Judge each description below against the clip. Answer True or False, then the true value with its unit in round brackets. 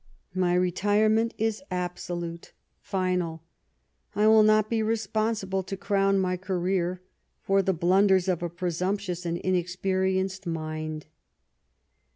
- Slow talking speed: True (115 wpm)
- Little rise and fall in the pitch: True (2.2 semitones)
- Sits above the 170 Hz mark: True (185 Hz)